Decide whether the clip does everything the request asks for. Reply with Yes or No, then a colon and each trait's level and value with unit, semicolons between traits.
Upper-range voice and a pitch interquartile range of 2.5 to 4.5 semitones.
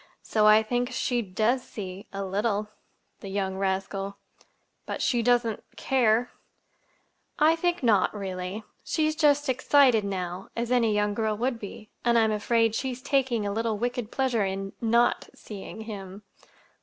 Yes: high, 220 Hz; average, 3.5 semitones